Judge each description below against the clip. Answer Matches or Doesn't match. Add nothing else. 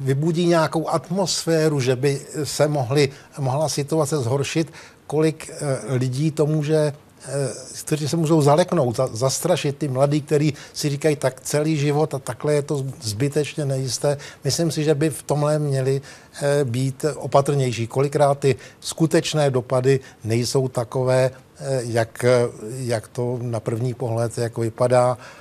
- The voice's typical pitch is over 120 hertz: Matches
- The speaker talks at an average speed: Matches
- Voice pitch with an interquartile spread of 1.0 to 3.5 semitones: Matches